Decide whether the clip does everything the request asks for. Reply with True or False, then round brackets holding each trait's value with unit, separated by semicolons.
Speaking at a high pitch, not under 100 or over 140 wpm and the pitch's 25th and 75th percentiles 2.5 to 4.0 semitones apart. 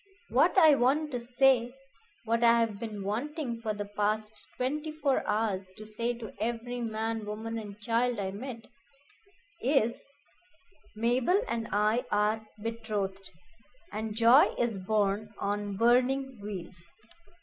True (225 Hz; 135 wpm; 2.8 semitones)